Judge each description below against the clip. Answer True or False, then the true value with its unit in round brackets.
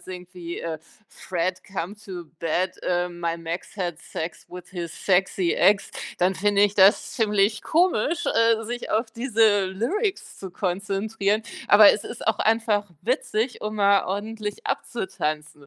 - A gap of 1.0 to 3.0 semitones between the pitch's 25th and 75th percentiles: False (3.5 semitones)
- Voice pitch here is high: True (200 Hz)